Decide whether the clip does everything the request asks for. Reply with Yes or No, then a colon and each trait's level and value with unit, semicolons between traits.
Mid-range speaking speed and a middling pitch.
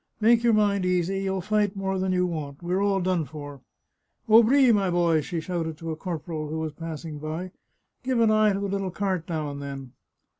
No: fast, 230 wpm; medium, 180 Hz